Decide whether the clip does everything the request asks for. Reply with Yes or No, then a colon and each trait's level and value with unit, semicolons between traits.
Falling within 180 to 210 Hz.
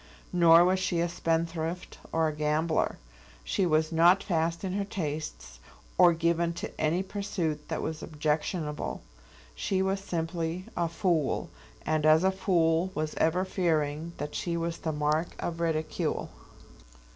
No: medium, 165 Hz